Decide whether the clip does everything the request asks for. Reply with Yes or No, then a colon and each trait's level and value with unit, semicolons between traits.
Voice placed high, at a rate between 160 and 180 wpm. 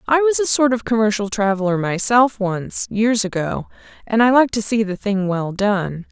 Yes: high, 215 Hz; average, 175 wpm